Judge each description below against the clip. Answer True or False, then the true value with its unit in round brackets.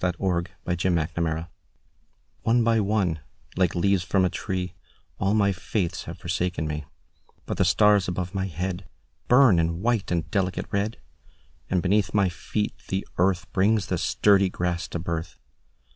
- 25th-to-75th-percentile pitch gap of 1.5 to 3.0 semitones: True (2.7 semitones)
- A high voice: False (90 Hz)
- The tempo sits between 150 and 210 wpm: False (140 wpm)